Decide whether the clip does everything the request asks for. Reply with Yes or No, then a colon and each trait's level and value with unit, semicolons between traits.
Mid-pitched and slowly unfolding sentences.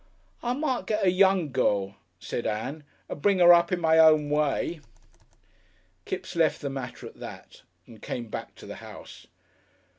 No: medium, 160 Hz; average, 170 wpm